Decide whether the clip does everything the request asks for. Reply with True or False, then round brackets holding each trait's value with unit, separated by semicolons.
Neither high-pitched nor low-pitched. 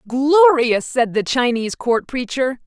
False (255 Hz)